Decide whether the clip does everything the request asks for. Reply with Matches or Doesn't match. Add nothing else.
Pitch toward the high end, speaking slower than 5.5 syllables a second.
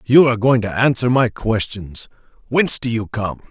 Doesn't match